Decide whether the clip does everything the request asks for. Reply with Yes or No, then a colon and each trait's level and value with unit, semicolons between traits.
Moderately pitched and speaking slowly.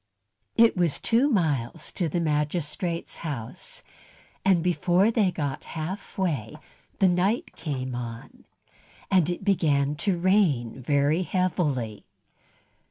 Yes: medium, 170 Hz; slow, 120 wpm